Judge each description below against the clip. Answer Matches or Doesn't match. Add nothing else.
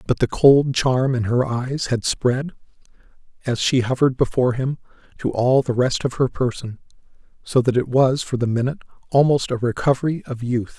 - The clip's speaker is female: Doesn't match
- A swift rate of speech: Doesn't match